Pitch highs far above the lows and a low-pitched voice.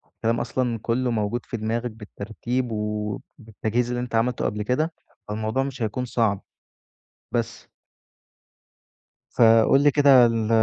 No: narrow, 2.4 semitones; low, 115 Hz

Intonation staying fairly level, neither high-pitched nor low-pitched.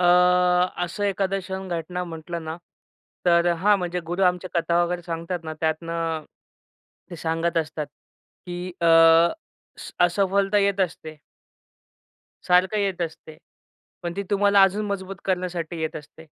Yes: narrow, 2.3 semitones; medium, 175 Hz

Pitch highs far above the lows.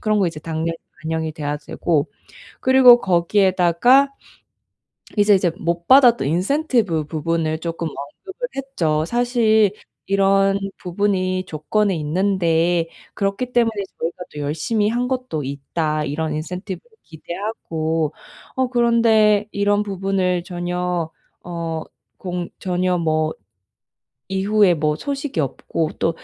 No: average, 4.8 semitones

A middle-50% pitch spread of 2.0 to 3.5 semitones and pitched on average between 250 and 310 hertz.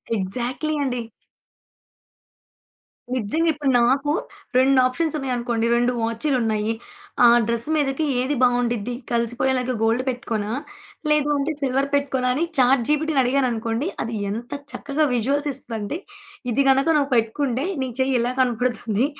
Yes: average, 2.9 semitones; very high, 255 Hz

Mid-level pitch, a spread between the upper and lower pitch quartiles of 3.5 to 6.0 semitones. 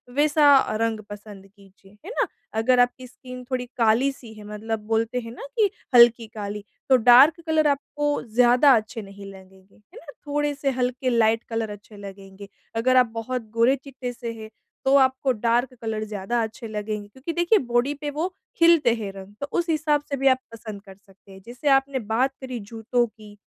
No: high, 235 Hz; average, 4.1 semitones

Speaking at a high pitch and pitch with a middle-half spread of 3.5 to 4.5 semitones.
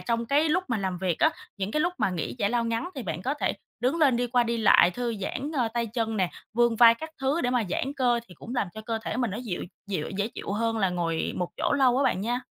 Yes: high, 235 Hz; average, 3.9 semitones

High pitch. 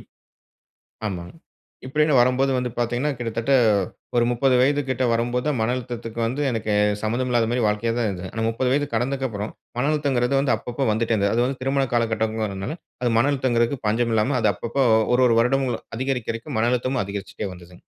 No: low, 120 Hz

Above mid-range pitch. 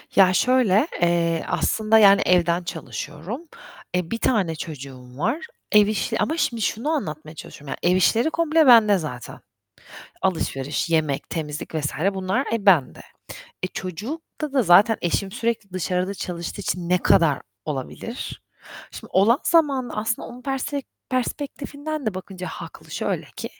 Yes: high, 195 Hz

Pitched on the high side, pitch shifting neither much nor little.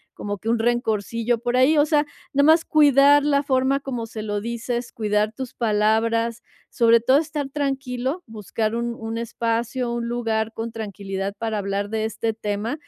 Yes: high, 235 Hz; average, 3.1 semitones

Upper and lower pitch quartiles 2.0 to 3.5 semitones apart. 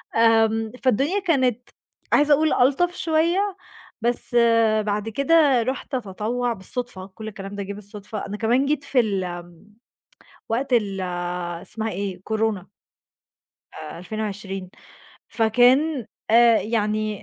No: average, 4.1 semitones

